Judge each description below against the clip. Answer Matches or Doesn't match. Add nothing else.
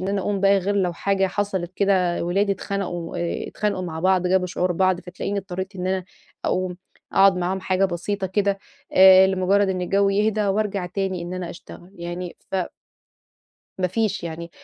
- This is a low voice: Doesn't match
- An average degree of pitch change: Doesn't match